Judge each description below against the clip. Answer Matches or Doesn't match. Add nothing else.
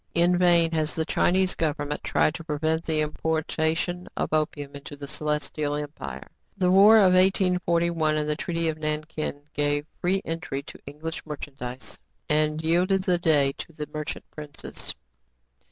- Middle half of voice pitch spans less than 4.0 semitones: Matches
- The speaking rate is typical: Matches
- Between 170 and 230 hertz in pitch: Doesn't match